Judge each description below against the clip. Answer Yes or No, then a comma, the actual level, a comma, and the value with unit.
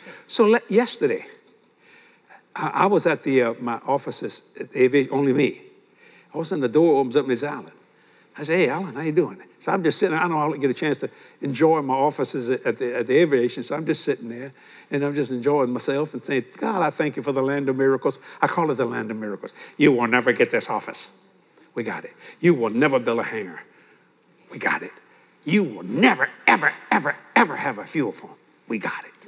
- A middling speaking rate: No, fast, 225 wpm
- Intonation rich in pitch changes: No, average, 4.1 semitones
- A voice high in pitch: No, medium, 140 Hz